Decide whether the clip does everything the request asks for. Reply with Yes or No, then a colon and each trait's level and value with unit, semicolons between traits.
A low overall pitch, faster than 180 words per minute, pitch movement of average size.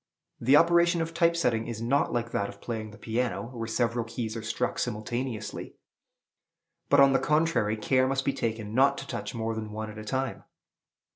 Yes: low, 120 Hz; average, 195 wpm; average, 3.5 semitones